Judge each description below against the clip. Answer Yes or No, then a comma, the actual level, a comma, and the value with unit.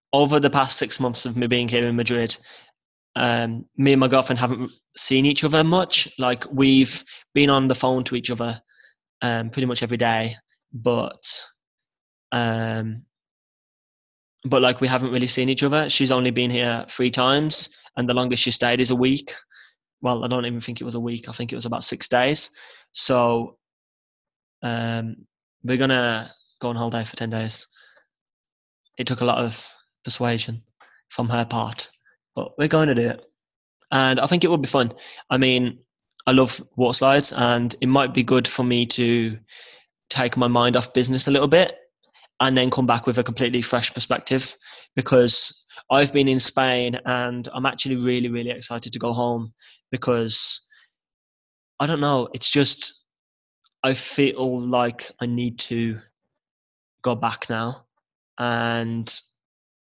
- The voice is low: Yes, low, 125 Hz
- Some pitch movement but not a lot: No, narrow, 1.8 semitones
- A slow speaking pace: No, average, 170 wpm